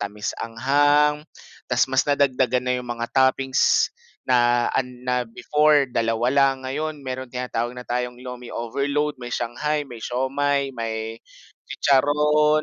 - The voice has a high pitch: No, low, 130 Hz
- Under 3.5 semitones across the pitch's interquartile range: Yes, average, 2.8 semitones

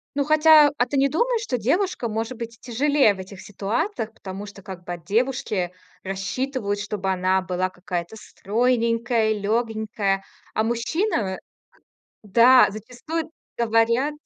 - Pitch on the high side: Yes, high, 225 Hz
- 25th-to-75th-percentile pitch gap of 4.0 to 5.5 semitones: Yes, average, 4.7 semitones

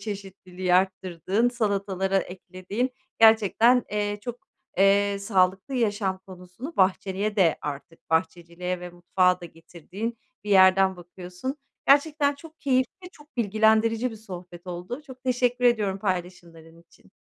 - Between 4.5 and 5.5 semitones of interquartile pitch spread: No, average, 4.0 semitones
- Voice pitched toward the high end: Yes, high, 195 Hz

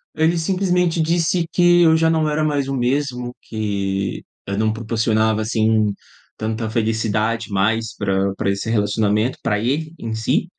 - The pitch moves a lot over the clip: Yes, wide, 6.2 semitones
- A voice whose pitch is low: Yes, low, 115 Hz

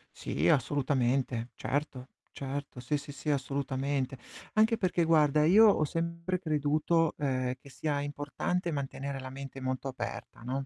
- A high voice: No, medium, 145 Hz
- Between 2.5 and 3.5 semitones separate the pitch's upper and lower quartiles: Yes, average, 2.8 semitones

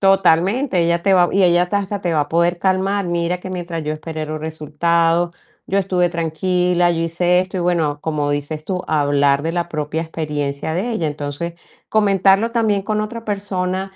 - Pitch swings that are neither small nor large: Yes, average, 3.2 semitones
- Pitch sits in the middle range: Yes, medium, 175 Hz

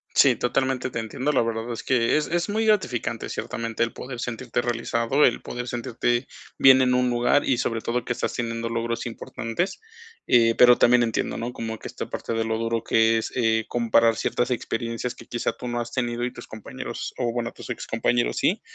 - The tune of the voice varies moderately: No, narrow, 1.4 semitones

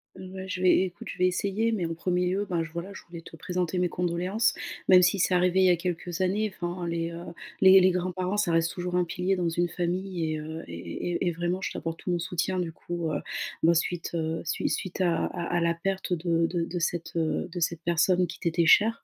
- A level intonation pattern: Yes, narrow, 1.7 semitones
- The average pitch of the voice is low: No, medium, 175 Hz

